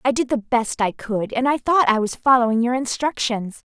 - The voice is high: Yes, high, 240 Hz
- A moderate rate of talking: No, fast, 220 wpm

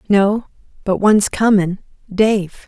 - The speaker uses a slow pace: Yes, slow, 90 wpm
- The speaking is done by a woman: Yes, female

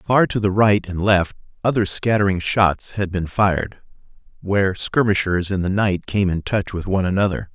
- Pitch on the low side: Yes, very low, 95 Hz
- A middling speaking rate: Yes, average, 185 wpm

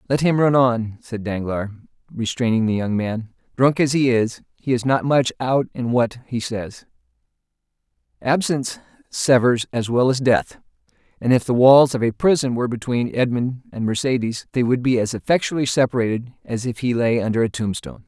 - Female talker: No, male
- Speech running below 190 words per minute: Yes, average, 180 wpm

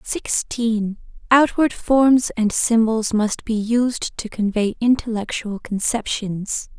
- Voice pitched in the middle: No, high, 225 Hz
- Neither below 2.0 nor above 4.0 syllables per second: Yes, 3.4 syllables/s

